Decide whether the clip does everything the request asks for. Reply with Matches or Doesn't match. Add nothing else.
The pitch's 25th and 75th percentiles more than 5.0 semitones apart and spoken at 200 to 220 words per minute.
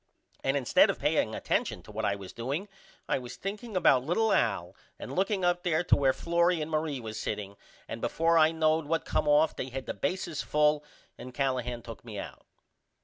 Matches